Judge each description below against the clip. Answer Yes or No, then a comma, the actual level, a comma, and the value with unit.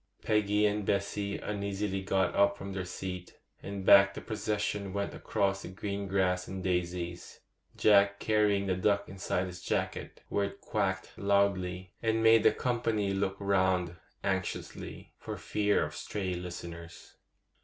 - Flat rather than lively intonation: Yes, narrow, 1.6 semitones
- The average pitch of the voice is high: No, low, 100 Hz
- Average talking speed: Yes, average, 145 wpm